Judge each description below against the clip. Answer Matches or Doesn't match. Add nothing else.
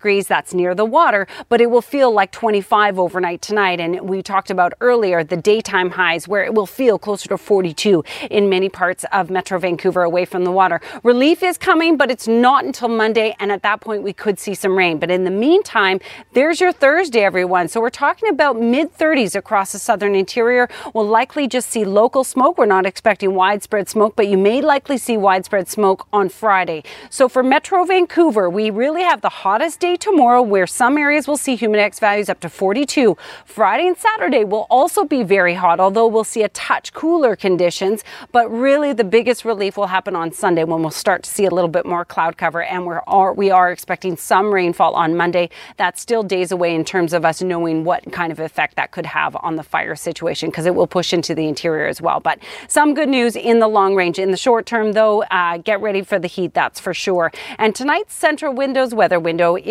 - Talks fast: Matches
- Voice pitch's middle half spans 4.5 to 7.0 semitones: Matches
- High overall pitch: Matches